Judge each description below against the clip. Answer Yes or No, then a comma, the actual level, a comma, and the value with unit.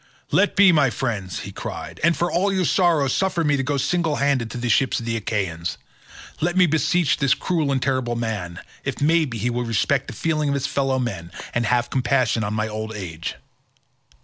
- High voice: No, low, 130 Hz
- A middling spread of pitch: No, wide, 5.7 semitones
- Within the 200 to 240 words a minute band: Yes, fast, 205 wpm